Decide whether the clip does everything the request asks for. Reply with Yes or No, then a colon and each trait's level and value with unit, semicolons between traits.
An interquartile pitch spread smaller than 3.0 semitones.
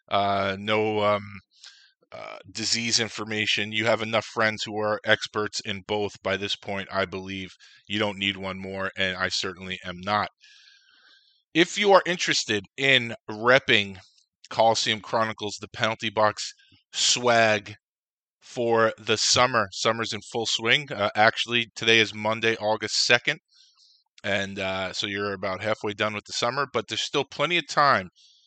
Yes: narrow, 2.4 semitones